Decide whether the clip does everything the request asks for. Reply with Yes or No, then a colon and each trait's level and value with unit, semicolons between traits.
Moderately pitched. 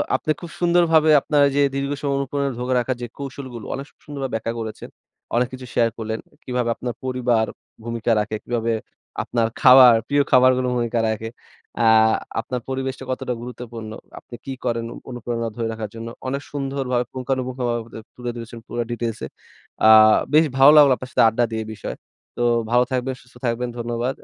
No: low, 125 Hz